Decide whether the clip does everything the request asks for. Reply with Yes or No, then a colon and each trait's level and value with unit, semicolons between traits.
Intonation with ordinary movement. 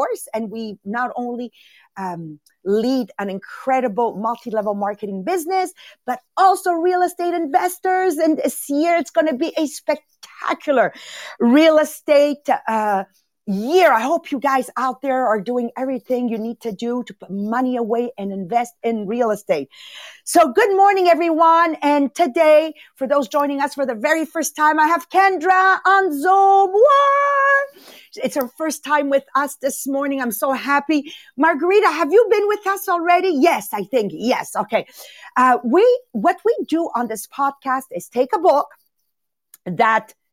No: wide, 5.9 semitones